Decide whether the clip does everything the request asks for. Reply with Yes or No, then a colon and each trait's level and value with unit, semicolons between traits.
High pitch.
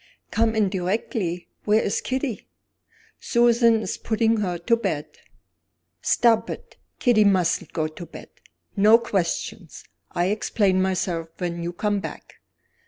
Yes: high, 205 Hz